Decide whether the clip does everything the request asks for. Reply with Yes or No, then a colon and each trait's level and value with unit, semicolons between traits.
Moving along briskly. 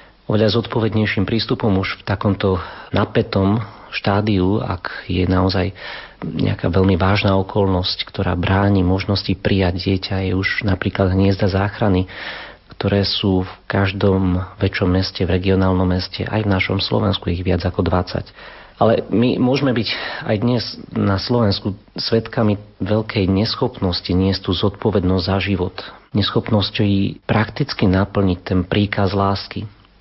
No: average, 130 wpm